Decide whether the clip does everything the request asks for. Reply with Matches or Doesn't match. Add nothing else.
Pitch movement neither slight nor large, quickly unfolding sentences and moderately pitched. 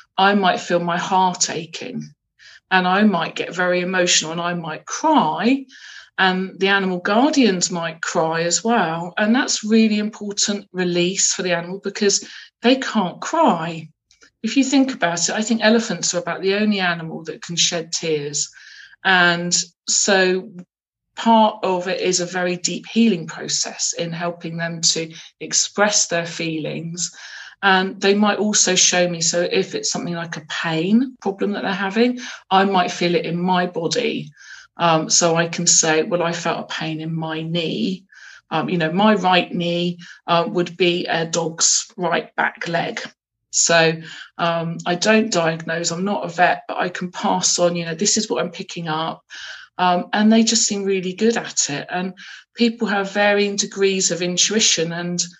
Doesn't match